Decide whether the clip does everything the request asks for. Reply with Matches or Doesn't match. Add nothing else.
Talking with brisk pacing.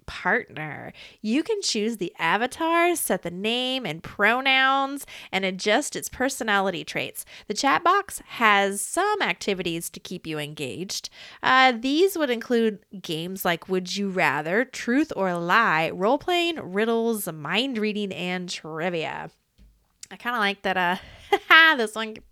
Doesn't match